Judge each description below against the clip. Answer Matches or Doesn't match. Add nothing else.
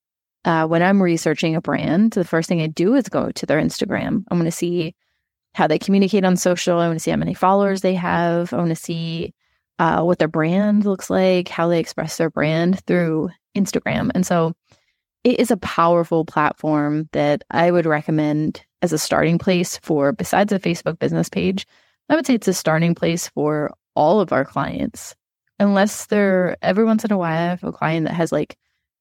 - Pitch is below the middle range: Doesn't match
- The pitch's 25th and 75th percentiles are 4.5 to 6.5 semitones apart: Doesn't match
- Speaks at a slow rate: Doesn't match